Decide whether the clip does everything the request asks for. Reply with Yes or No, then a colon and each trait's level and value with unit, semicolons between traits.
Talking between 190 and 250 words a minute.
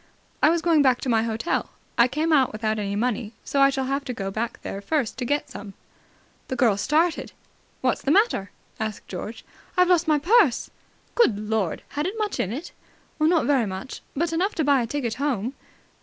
Yes: average, 200 wpm